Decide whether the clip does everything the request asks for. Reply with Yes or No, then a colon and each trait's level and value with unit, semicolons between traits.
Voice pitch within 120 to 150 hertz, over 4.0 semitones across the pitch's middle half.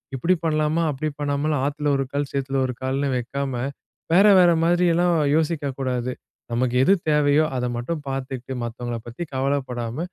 No: medium, 140 Hz; average, 3.3 semitones